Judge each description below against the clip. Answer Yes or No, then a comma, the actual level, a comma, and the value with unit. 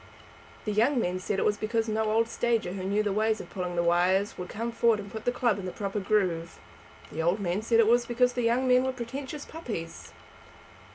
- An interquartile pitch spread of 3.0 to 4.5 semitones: Yes, average, 3.8 semitones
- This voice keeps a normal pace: No, fast, 230 wpm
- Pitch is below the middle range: No, high, 215 Hz